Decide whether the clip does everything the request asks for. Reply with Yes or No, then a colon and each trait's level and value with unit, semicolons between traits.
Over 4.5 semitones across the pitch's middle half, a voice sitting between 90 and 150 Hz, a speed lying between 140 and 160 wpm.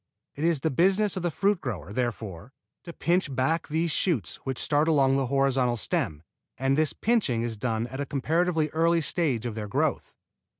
No: wide, 5.5 semitones; medium, 140 Hz; average, 185 wpm